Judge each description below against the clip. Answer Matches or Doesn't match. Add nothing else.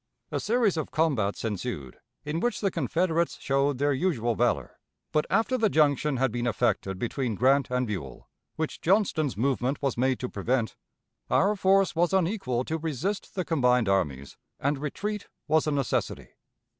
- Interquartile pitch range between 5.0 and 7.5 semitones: Matches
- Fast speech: Doesn't match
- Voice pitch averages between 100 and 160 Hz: Matches